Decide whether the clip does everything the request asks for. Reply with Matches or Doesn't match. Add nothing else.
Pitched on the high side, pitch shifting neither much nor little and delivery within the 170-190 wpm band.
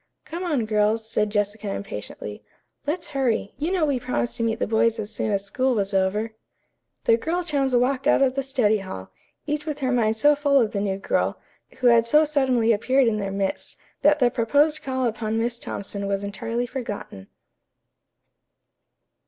Matches